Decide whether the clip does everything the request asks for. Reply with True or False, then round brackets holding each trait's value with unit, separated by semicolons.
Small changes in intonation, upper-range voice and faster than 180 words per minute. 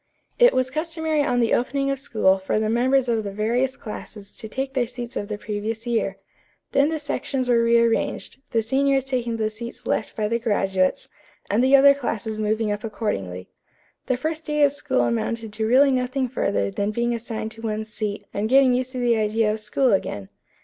False (3.5 semitones; 235 Hz; 200 wpm)